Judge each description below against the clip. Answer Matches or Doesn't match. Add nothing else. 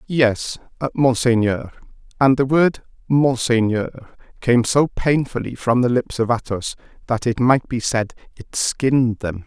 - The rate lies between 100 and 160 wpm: Matches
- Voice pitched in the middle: Doesn't match